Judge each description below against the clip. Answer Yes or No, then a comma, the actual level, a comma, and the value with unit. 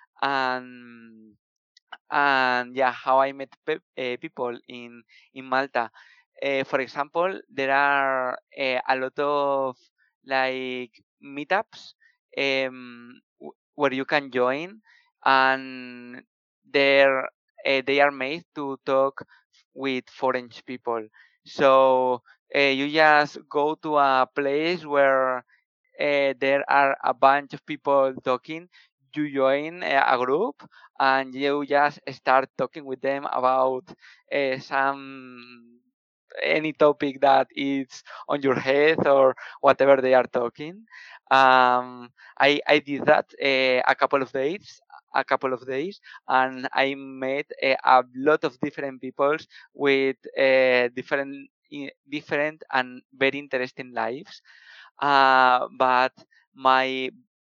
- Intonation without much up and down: Yes, narrow, 1.7 semitones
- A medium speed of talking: No, slow, 125 wpm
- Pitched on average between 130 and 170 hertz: Yes, low, 135 Hz